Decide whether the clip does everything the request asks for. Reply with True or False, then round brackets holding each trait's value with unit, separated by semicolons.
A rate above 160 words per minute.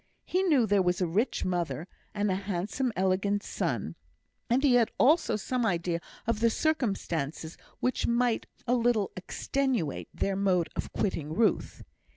False (155 wpm)